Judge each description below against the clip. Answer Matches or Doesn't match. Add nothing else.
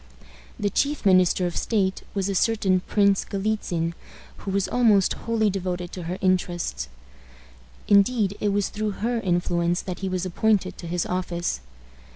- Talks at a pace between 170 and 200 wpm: Doesn't match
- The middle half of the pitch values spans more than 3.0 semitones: Doesn't match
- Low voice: Doesn't match